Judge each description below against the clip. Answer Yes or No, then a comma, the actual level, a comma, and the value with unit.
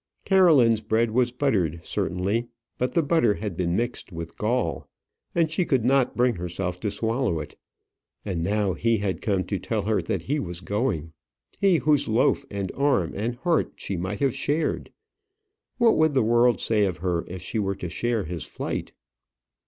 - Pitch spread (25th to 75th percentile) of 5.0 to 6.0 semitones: Yes, wide, 5.5 semitones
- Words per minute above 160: Yes, average, 180 wpm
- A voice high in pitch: No, low, 110 Hz